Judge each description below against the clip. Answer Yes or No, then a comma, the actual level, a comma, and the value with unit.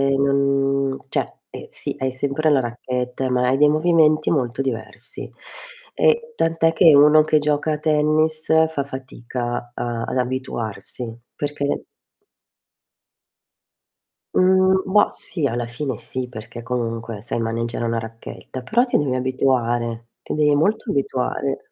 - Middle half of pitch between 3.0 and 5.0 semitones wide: Yes, average, 4.1 semitones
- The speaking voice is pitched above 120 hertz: Yes, low, 135 Hz